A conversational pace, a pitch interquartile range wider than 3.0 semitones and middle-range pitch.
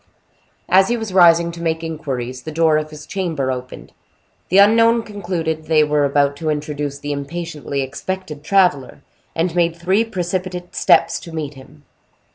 Yes: average, 160 wpm; average, 3.7 semitones; medium, 160 Hz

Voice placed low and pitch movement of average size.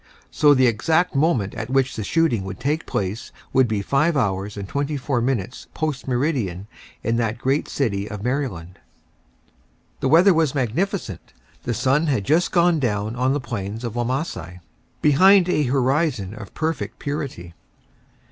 No: low, 130 Hz; wide, 6.1 semitones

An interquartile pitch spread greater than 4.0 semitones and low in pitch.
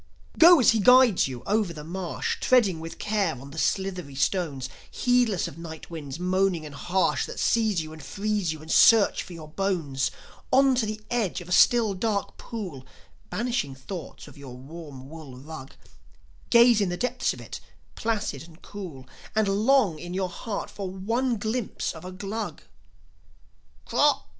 No: wide, 5.6 semitones; medium, 185 Hz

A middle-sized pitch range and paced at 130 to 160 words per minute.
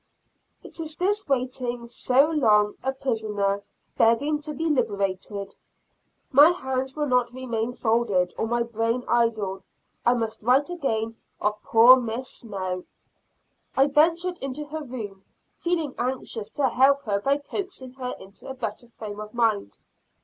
Yes: average, 4.1 semitones; average, 145 wpm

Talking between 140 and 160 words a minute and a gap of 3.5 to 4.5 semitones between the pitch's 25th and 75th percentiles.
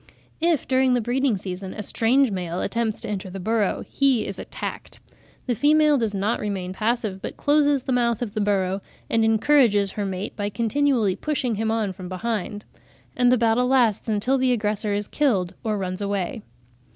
No: average, 185 wpm; average, 3.9 semitones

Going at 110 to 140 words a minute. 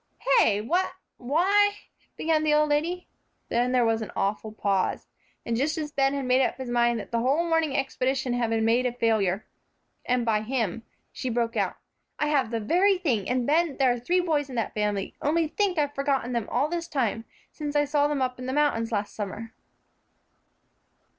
No: average, 200 wpm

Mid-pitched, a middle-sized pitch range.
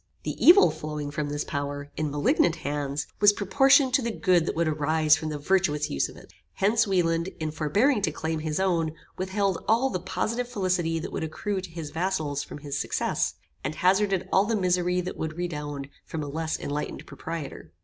Yes: medium, 165 Hz; average, 4.3 semitones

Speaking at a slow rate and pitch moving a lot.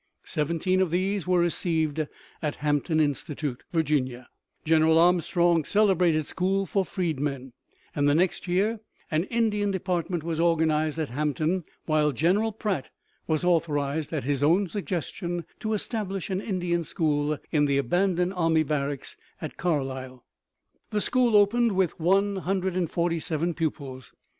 No: slow, 130 wpm; average, 3.8 semitones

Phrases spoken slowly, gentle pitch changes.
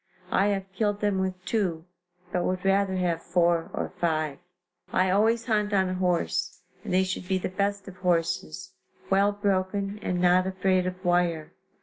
No: average, 175 wpm; narrow, 1.9 semitones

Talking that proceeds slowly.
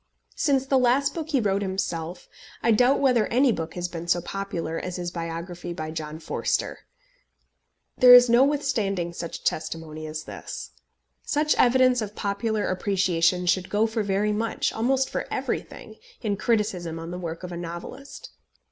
No: average, 165 wpm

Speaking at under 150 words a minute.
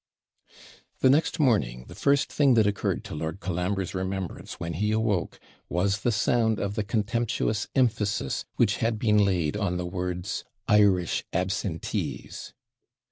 Yes: average, 140 wpm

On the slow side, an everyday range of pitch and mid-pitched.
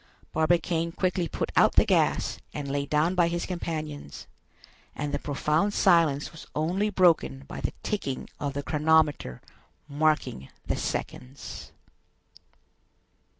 Yes: slow, 125 wpm; average, 3.2 semitones; medium, 155 Hz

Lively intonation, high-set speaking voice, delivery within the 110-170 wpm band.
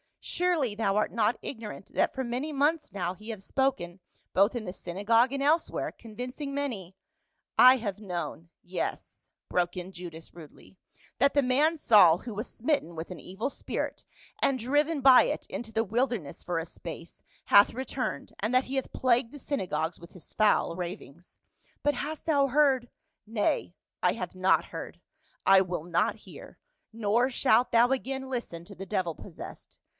No: wide, 6.6 semitones; high, 225 Hz; average, 190 wpm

